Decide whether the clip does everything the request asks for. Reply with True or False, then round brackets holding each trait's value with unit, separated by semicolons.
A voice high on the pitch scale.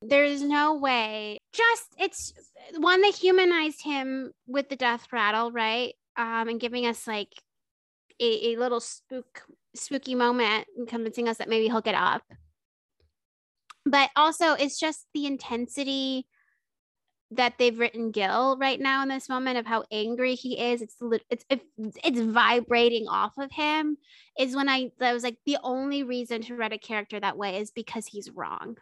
True (245 Hz)